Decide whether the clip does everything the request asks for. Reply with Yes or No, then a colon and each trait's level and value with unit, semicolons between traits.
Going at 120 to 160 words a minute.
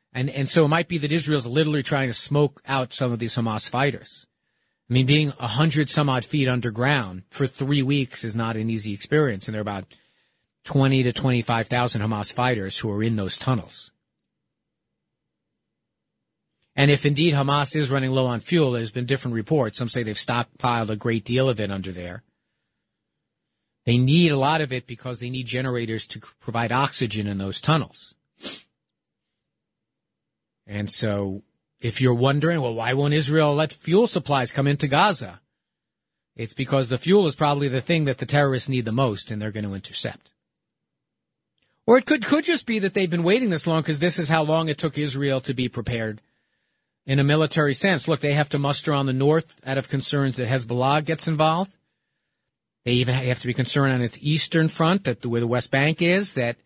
No: average, 195 wpm